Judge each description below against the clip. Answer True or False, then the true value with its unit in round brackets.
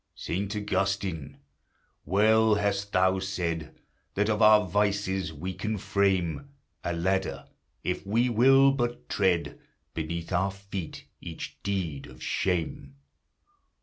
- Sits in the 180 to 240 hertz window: False (95 Hz)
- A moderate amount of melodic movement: True (3.1 semitones)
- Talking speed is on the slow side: True (115 wpm)